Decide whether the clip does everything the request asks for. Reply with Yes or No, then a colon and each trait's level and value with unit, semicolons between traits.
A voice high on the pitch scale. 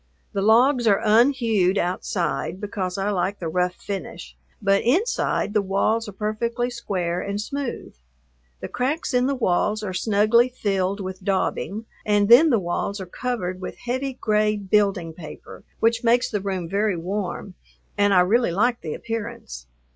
Yes: high, 205 Hz